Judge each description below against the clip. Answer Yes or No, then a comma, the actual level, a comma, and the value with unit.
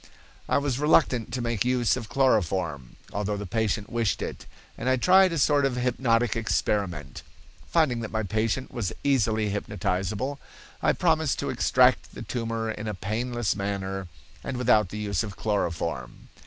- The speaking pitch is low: Yes, low, 110 Hz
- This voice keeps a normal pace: Yes, average, 155 wpm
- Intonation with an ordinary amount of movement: Yes, average, 3.7 semitones